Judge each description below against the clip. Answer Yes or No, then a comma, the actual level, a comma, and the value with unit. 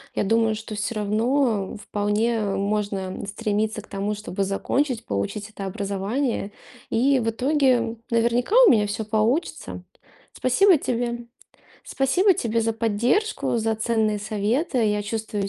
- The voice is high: Yes, high, 220 Hz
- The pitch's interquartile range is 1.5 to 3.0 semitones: Yes, average, 2.7 semitones